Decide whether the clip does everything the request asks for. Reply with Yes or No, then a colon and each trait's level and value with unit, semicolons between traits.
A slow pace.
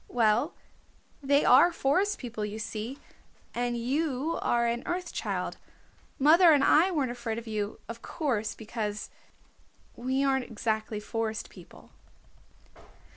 Yes: slow, 130 wpm